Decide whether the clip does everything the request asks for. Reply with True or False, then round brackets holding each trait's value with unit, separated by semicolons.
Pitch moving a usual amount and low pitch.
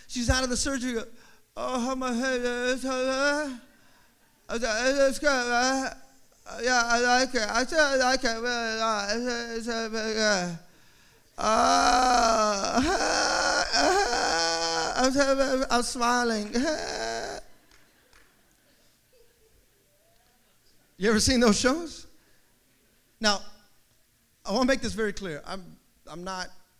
False (3.1 semitones; 240 Hz)